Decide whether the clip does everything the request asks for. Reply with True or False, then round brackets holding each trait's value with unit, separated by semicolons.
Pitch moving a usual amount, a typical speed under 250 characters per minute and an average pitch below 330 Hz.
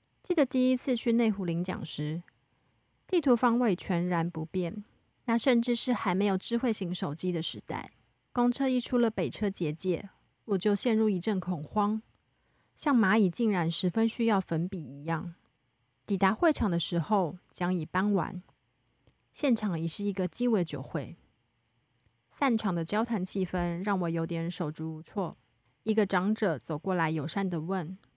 True (4.9 semitones; 235 characters per minute; 185 Hz)